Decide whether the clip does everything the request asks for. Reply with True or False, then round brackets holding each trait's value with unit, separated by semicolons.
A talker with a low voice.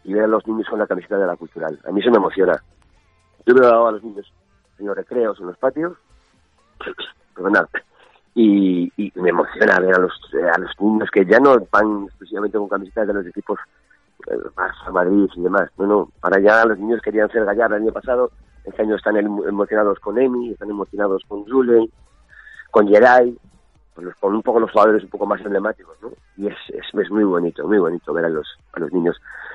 True (105 Hz)